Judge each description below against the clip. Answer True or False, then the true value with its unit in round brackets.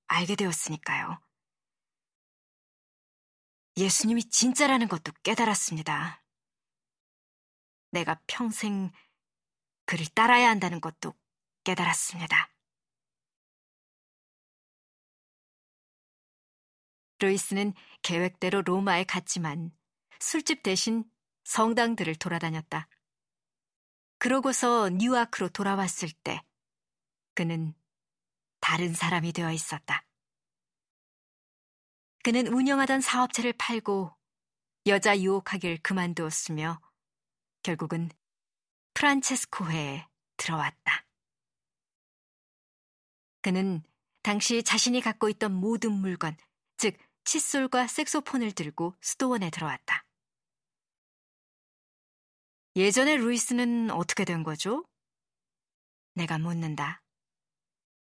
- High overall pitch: True (195 Hz)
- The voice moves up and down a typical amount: False (5.8 semitones)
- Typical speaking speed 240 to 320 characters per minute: False (190 characters per minute)